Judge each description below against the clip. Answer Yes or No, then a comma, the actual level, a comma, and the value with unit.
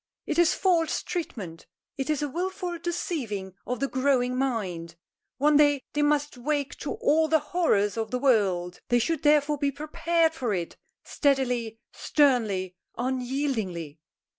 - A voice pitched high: Yes, very high, 270 Hz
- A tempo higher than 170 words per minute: No, average, 145 wpm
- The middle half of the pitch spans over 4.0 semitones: Yes, average, 5.2 semitones